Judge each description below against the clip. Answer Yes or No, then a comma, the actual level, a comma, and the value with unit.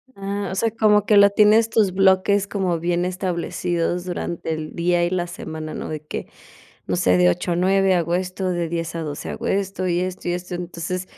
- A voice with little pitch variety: Yes, narrow, 2.2 semitones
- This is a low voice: No, medium, 180 Hz